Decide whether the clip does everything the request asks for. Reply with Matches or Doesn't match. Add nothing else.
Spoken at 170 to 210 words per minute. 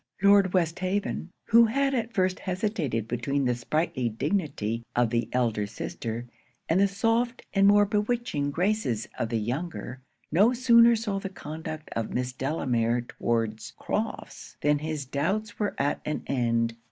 Doesn't match